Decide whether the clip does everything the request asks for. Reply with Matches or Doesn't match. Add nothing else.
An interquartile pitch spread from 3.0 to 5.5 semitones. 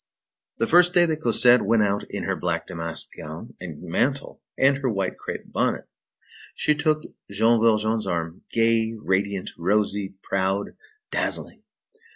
Matches